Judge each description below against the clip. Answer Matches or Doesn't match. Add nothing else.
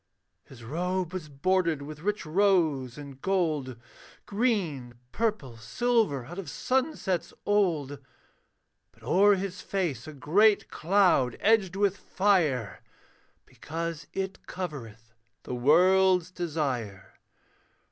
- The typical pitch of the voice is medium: Matches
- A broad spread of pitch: Matches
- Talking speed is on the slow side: Matches